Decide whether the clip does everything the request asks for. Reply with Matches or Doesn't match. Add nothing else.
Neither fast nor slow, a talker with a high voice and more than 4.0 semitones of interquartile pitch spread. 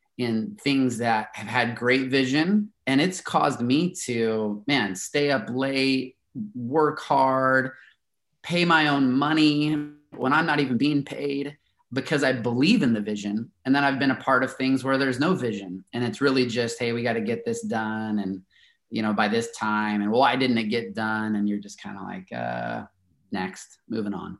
Doesn't match